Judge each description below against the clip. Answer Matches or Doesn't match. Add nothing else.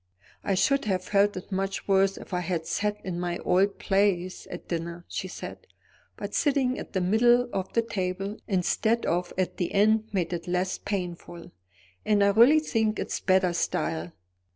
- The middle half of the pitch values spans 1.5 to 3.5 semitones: Matches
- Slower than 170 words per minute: Doesn't match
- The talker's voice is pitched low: Doesn't match